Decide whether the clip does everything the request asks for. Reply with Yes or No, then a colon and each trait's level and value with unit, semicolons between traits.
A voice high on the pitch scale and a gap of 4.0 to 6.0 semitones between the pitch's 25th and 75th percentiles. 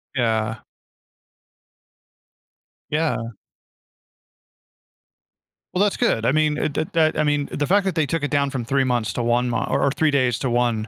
No: medium, 140 Hz; average, 4.3 semitones